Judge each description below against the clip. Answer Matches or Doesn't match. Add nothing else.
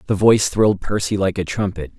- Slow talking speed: Doesn't match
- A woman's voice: Doesn't match